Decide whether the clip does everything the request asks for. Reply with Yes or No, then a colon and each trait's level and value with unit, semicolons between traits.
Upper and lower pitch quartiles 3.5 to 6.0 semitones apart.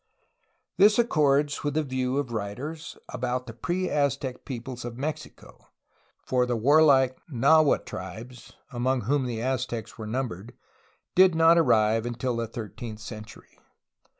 Yes: average, 3.9 semitones